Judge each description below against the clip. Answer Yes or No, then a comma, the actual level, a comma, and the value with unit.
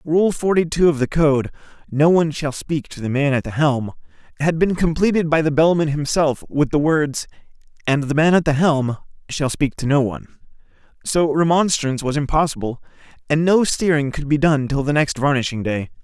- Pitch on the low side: No, medium, 150 Hz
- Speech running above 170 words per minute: Yes, average, 195 wpm